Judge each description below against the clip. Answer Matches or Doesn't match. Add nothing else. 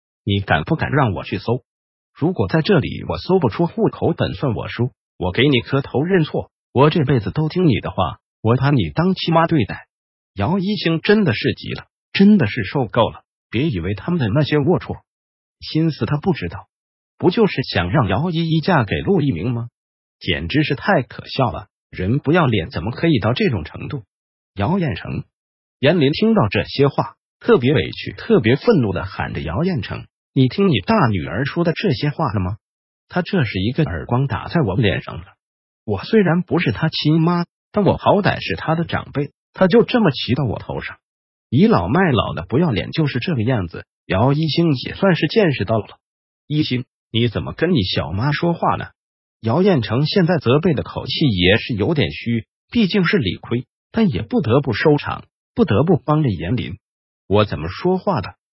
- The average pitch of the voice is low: Doesn't match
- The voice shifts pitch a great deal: Matches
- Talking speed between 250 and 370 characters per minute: Matches